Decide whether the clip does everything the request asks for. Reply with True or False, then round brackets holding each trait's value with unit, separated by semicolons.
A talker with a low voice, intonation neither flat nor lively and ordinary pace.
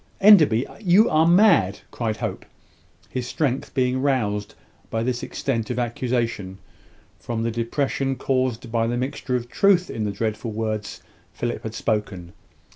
True (120 Hz; 3.4 semitones; 150 wpm)